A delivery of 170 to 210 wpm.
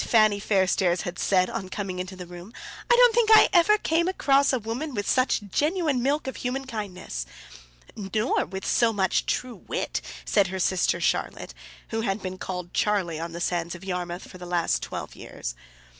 Yes: average, 190 wpm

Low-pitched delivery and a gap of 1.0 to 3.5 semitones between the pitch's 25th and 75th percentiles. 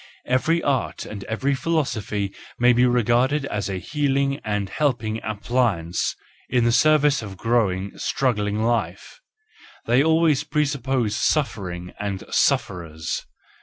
No: low, 120 Hz; average, 5.2 semitones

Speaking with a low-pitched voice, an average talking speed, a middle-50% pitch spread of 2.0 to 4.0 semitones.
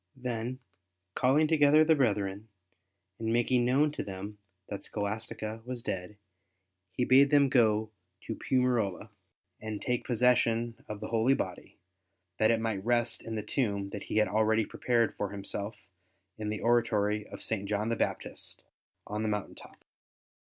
Yes: low, 110 Hz; average, 155 wpm; average, 2.8 semitones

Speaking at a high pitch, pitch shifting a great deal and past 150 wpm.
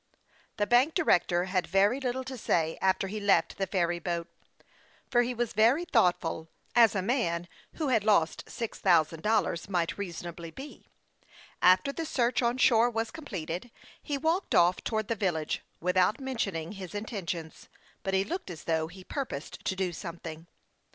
Yes: high, 195 Hz; wide, 5.8 semitones; average, 175 wpm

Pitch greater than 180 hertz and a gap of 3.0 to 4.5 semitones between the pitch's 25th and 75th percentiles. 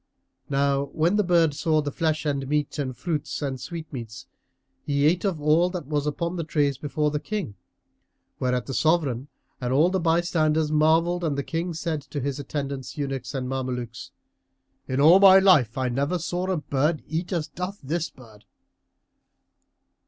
No: medium, 150 Hz; average, 3.6 semitones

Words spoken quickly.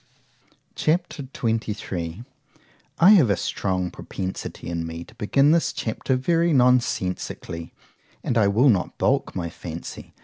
No: average, 145 wpm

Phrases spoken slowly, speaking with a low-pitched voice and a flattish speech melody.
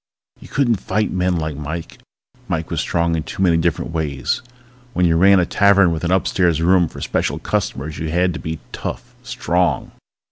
No: average, 185 wpm; very low, 85 Hz; narrow, 2.3 semitones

